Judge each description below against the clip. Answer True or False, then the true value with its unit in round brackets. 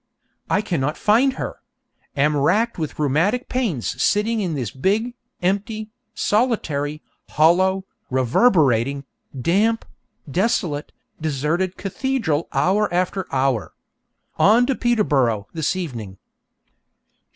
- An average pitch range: False (7.0 semitones)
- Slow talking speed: True (100 wpm)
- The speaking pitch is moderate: True (175 Hz)